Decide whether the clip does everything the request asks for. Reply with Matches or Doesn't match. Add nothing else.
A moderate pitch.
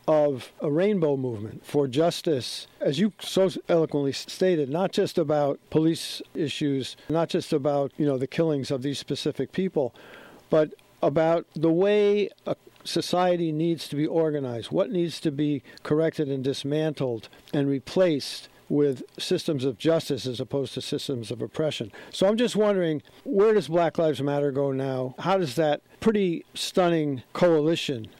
Matches